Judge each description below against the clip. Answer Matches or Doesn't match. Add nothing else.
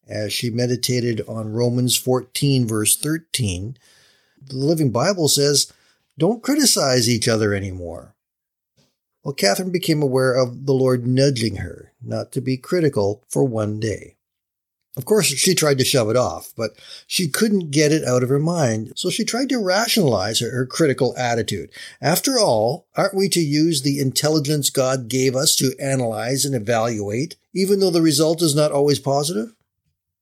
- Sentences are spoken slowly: Doesn't match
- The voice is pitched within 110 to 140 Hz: Matches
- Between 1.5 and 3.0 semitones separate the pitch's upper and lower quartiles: Doesn't match